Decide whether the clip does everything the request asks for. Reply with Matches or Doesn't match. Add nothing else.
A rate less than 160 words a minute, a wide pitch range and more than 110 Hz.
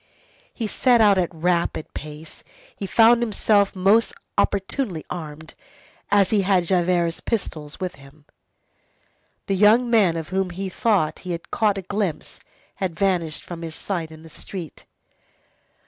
Doesn't match